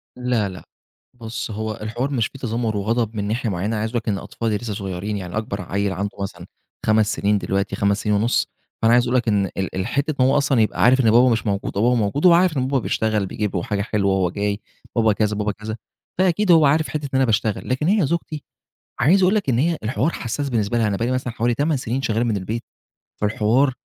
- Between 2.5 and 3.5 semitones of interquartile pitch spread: No, average, 3.9 semitones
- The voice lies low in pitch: Yes, low, 115 Hz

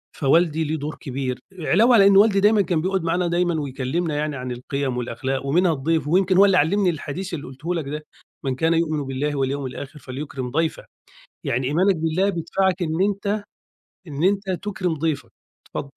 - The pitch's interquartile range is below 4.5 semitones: No, average, 4.8 semitones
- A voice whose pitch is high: No, medium, 160 Hz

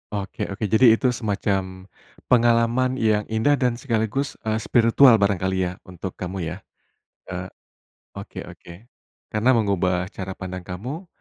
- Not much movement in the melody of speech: No, average, 4.1 semitones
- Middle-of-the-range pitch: No, low, 110 Hz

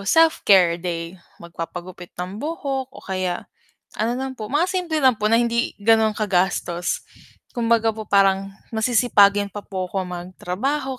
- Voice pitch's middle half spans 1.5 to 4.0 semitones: No, average, 5.0 semitones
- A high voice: Yes, high, 210 Hz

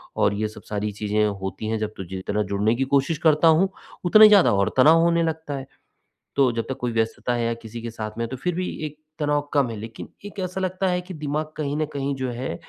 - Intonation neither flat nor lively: No, wide, 6.6 semitones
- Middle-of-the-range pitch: No, low, 130 Hz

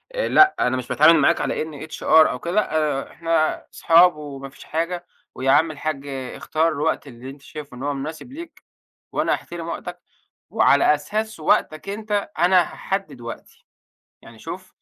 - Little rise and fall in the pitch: No, average, 4.2 semitones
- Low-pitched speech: No, medium, 155 Hz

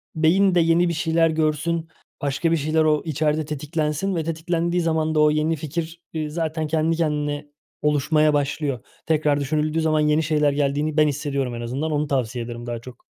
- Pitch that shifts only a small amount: Yes, narrow, 1.7 semitones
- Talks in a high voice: No, medium, 155 Hz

